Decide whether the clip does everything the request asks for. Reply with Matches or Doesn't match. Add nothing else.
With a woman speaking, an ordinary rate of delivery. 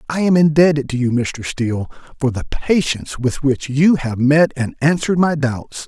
Doesn't match